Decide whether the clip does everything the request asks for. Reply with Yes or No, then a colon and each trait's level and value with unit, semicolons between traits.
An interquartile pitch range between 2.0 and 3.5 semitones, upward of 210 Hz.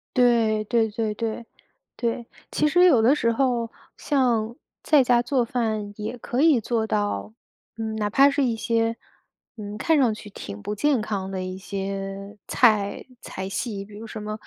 Yes: average, 2.8 semitones; high, 220 Hz